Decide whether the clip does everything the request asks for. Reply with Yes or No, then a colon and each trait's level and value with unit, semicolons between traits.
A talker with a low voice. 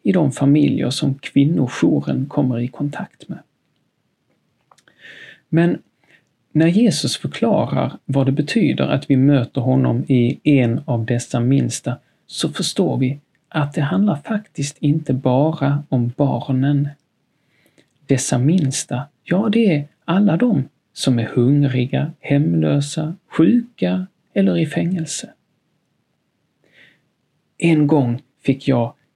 No: medium, 145 Hz